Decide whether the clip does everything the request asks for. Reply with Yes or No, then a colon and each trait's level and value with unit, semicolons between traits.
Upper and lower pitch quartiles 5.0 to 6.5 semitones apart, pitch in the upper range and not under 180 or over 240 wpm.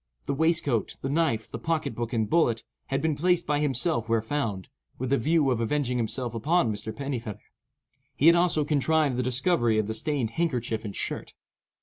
No: wide, 5.4 semitones; low, 135 Hz; average, 190 wpm